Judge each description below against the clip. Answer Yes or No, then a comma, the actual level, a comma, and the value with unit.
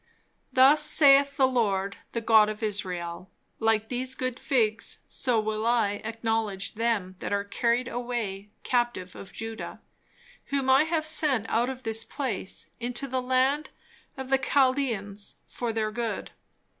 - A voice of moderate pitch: No, high, 230 Hz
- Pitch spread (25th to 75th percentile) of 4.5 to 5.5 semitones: No, average, 3.4 semitones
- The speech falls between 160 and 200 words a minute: No, average, 145 wpm